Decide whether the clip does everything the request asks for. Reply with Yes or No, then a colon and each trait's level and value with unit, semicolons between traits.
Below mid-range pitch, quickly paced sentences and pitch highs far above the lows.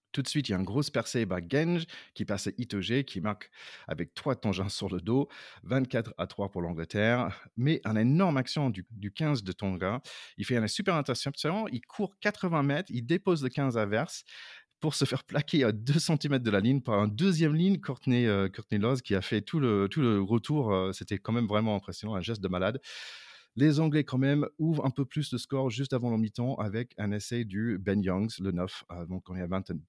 Yes: low, 120 Hz; fast, 235 wpm; wide, 5.9 semitones